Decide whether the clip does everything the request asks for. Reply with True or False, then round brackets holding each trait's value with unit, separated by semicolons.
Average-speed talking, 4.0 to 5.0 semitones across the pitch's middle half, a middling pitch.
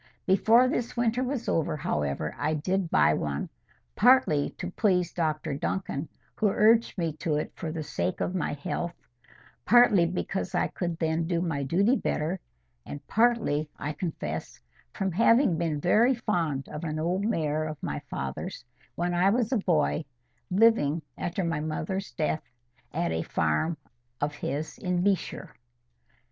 True (155 wpm; 4.6 semitones; 170 Hz)